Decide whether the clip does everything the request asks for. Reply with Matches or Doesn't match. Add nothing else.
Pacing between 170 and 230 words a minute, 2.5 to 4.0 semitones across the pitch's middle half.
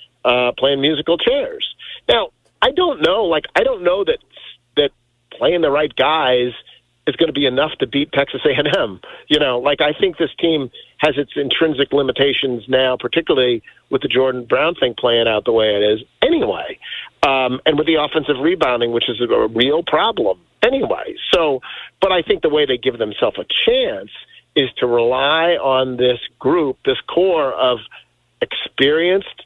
Doesn't match